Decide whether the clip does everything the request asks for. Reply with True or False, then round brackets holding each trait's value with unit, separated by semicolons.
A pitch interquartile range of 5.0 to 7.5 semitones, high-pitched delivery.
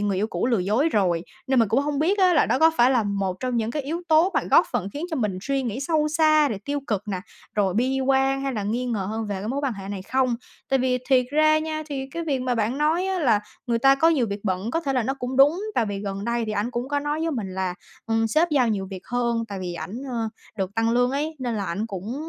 True (5.4 semitones; 245 Hz)